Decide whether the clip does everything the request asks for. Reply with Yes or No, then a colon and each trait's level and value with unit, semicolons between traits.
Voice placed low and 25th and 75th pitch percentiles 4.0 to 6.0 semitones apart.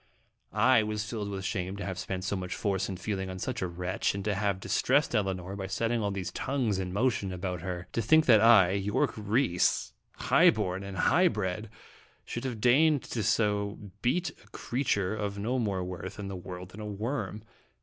No: low, 100 Hz; average, 3.3 semitones